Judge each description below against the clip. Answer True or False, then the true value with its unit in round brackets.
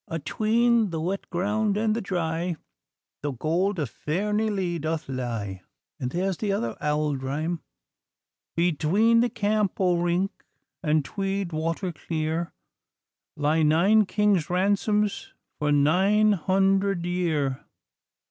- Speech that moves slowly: True (120 wpm)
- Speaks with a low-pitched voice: False (175 Hz)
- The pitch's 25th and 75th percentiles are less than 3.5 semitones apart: False (4.5 semitones)